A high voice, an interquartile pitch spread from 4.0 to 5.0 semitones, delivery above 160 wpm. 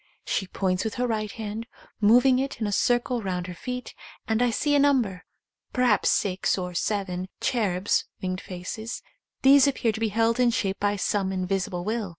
Yes: high, 215 Hz; average, 4.3 semitones; average, 180 wpm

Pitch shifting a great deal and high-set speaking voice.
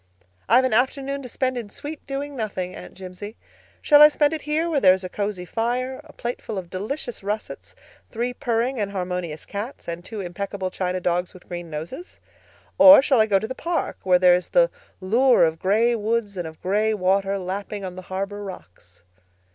Yes: wide, 5.7 semitones; high, 205 Hz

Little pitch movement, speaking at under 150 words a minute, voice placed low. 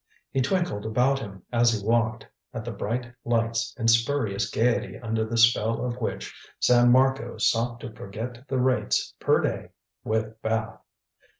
No: narrow, 1.8 semitones; average, 160 wpm; low, 115 Hz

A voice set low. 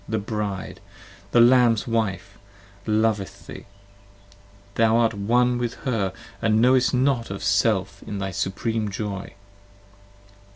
Yes: low, 110 Hz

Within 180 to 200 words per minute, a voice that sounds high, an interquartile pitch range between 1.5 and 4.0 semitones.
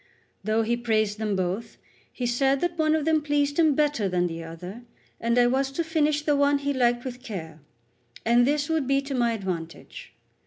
No: average, 195 wpm; high, 245 Hz; average, 5.0 semitones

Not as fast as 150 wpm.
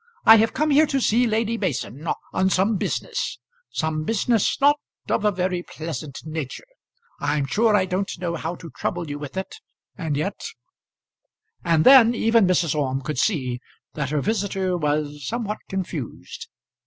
No: average, 165 wpm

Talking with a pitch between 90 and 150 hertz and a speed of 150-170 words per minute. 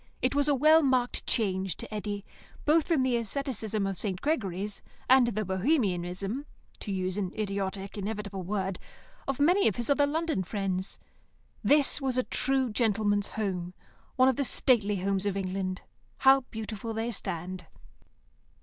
No: high, 210 Hz; average, 155 wpm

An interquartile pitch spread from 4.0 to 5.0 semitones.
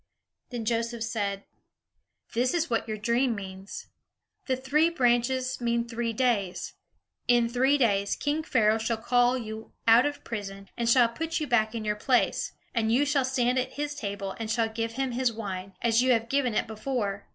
No: average, 2.8 semitones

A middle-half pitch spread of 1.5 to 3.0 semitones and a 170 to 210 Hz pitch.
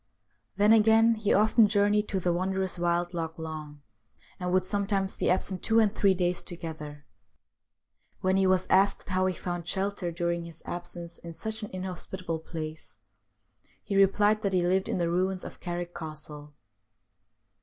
Yes: narrow, 2.5 semitones; medium, 185 Hz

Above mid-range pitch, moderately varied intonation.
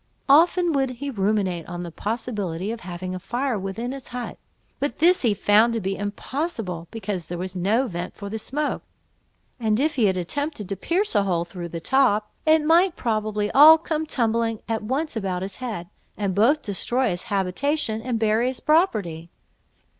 No: high, 220 Hz; wide, 6.1 semitones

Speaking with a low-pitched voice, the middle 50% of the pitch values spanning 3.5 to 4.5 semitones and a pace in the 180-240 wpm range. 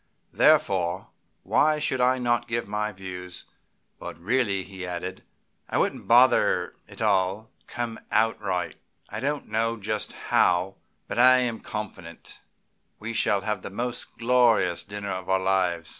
No: low, 105 Hz; average, 4.0 semitones; average, 145 wpm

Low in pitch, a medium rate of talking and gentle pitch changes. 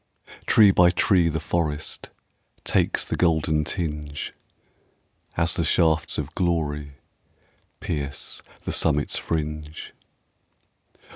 No: very low, 80 Hz; slow, 95 wpm; narrow, 2.3 semitones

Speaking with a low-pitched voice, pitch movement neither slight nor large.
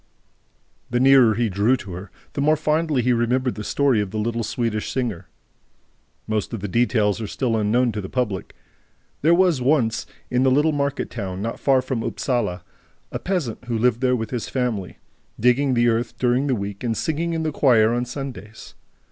Yes: low, 120 Hz; average, 3.6 semitones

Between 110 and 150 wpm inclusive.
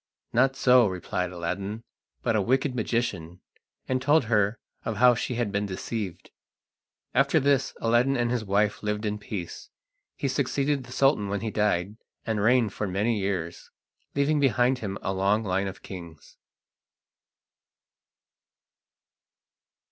Yes: average, 140 wpm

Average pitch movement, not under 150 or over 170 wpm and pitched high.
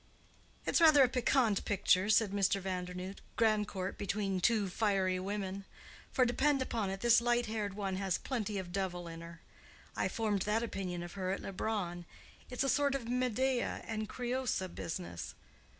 Yes: average, 4.0 semitones; average, 160 wpm; high, 205 Hz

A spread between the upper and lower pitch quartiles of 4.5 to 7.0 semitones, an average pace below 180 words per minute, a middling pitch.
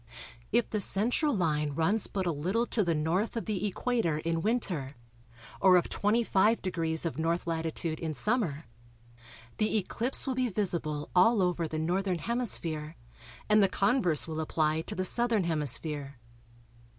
Yes: average, 5.1 semitones; average, 150 wpm; medium, 180 Hz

